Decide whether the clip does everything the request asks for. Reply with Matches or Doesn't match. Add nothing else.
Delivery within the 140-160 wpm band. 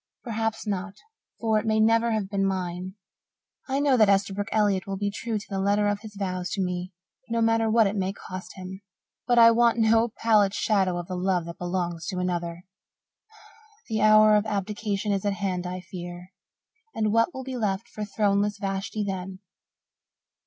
Doesn't match